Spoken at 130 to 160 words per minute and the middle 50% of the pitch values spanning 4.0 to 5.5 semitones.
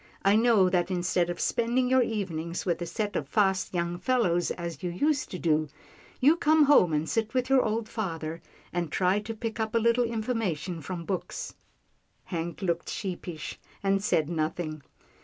No: average, 175 wpm; average, 4.9 semitones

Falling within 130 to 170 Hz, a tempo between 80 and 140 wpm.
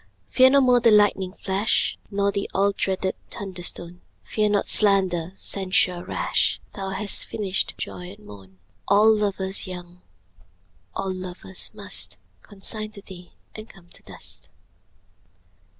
No: high, 195 Hz; slow, 135 wpm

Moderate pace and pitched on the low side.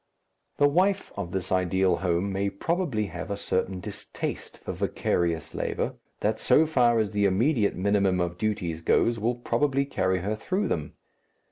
Yes: average, 160 wpm; low, 100 Hz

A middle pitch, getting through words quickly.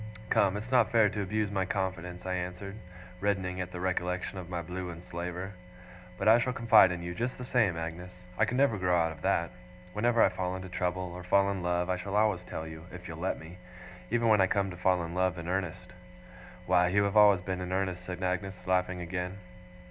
No: very low, 90 Hz; fast, 225 wpm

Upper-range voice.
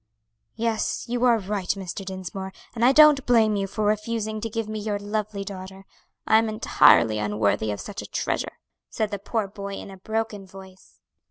Yes: high, 205 Hz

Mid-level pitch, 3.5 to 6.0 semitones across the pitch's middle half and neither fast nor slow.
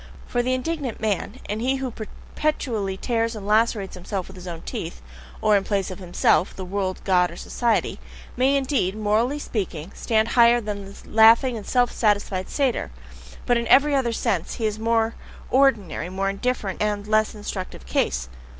No: high, 215 Hz; average, 3.8 semitones; average, 180 wpm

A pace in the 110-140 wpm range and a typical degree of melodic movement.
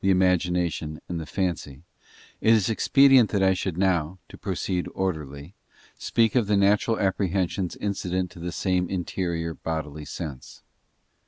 Yes: slow, 135 wpm; average, 3.0 semitones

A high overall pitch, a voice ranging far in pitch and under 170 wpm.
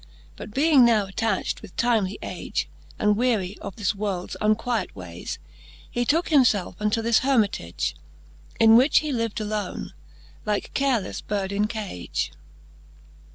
No: high, 215 Hz; average, 3.2 semitones; average, 140 wpm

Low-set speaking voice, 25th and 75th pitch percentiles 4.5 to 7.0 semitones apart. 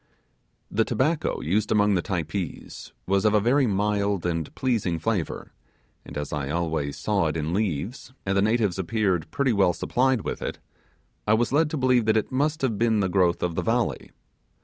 Yes: low, 105 Hz; average, 5.2 semitones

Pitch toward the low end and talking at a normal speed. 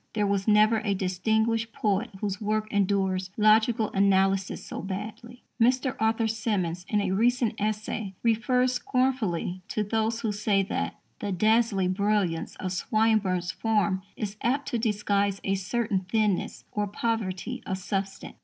No: high, 210 Hz; average, 145 wpm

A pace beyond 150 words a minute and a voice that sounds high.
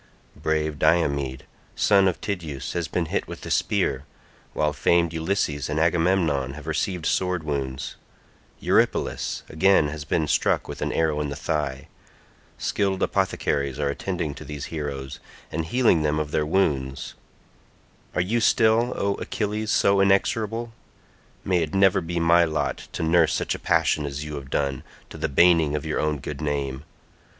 No: average, 160 wpm; very low, 80 Hz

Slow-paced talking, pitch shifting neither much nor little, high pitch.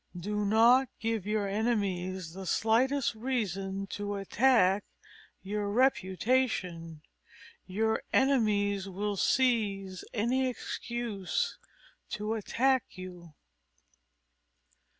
Yes: slow, 85 wpm; average, 3.7 semitones; high, 210 Hz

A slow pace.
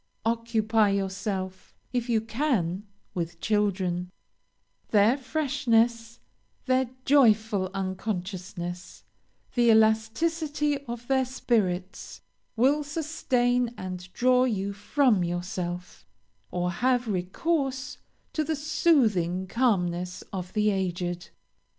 Yes: slow, 95 wpm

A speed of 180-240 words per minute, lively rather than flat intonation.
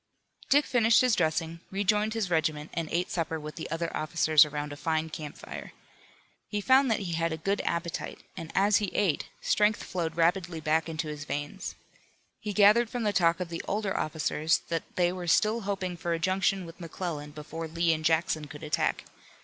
No: average, 195 wpm; average, 3.8 semitones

